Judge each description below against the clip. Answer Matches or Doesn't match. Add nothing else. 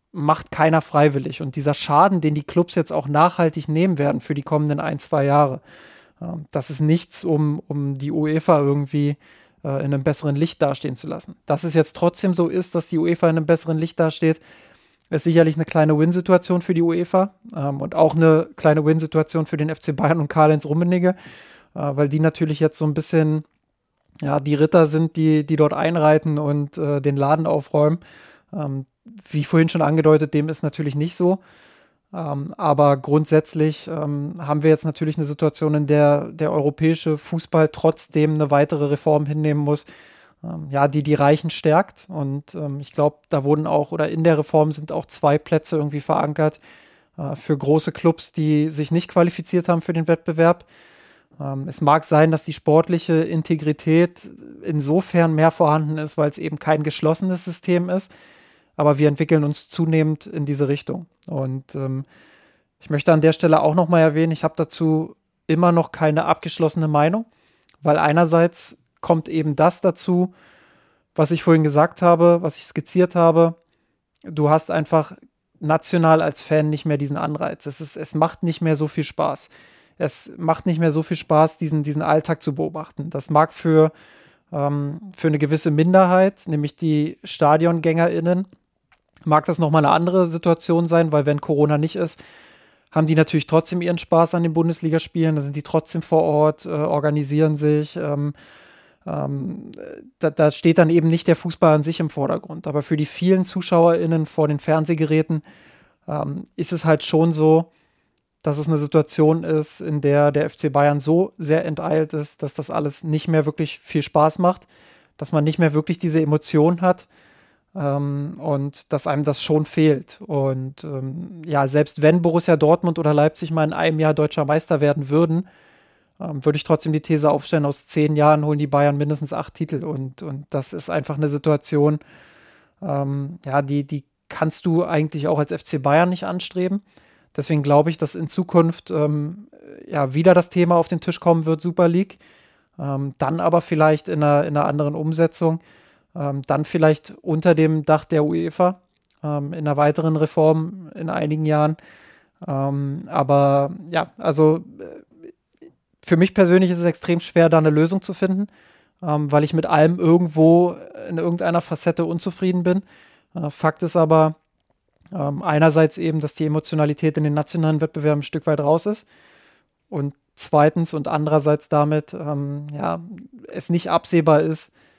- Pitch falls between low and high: Matches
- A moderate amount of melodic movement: Doesn't match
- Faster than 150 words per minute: Matches